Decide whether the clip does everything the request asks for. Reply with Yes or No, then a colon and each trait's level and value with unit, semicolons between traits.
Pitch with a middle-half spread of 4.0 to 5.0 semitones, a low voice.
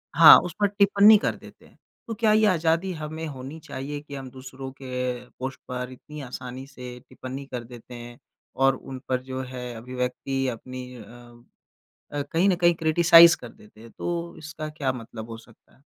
Yes: average, 4.4 semitones; low, 130 Hz